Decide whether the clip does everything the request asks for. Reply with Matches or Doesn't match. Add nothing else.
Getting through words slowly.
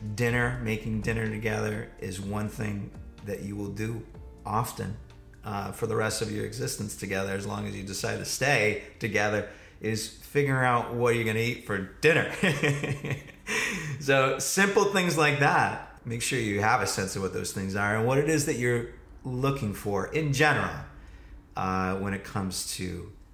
Doesn't match